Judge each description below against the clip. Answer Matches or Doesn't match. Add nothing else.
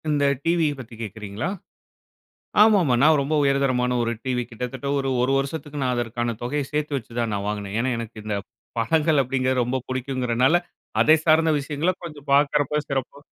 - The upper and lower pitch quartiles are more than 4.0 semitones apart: Doesn't match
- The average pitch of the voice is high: Doesn't match